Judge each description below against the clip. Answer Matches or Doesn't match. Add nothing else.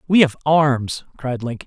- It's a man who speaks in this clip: Matches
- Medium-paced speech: Matches